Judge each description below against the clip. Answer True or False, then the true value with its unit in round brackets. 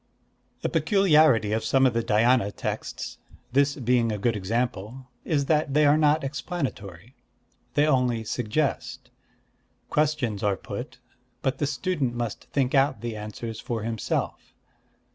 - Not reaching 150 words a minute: True (140 wpm)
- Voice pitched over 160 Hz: False (125 Hz)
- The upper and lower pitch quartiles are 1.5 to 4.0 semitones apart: False (4.5 semitones)